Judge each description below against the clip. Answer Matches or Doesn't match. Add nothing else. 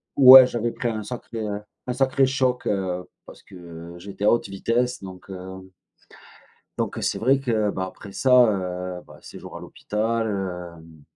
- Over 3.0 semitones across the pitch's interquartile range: Matches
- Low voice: Matches